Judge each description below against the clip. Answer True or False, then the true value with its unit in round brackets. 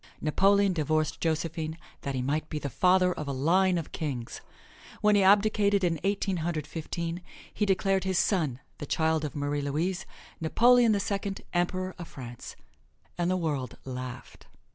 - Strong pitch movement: False (4.3 semitones)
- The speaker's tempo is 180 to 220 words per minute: False (165 wpm)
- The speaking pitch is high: False (170 Hz)